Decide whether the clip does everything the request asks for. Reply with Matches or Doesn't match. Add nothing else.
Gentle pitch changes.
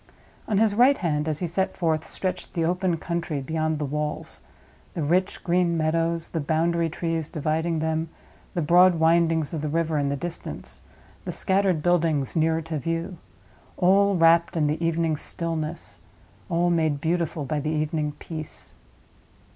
Matches